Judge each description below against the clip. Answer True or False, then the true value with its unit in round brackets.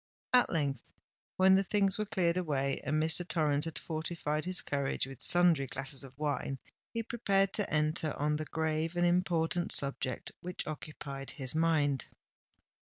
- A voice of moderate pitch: True (155 Hz)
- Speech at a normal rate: True (155 wpm)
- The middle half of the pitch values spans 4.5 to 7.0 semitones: False (3.7 semitones)